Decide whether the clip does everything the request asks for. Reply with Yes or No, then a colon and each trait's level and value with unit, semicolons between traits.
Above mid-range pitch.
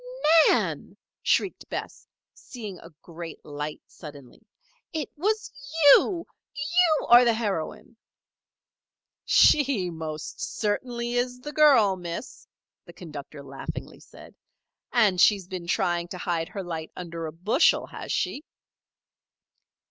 Yes: high, 195 Hz